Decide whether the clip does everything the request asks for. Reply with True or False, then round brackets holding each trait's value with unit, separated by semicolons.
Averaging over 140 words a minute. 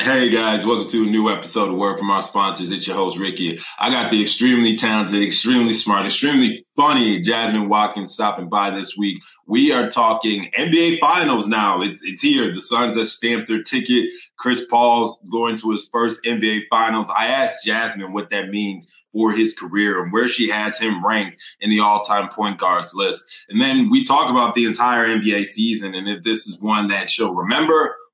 True (200 wpm)